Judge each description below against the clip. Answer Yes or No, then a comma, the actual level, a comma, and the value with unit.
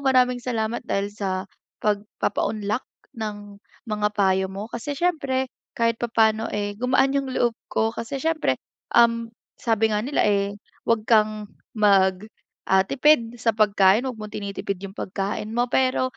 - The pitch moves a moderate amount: Yes, average, 3.1 semitones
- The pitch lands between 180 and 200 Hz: No, high, 220 Hz